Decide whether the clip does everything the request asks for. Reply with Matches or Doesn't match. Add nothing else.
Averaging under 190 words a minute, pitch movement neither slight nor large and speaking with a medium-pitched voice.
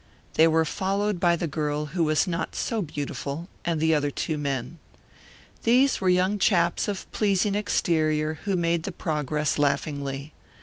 Matches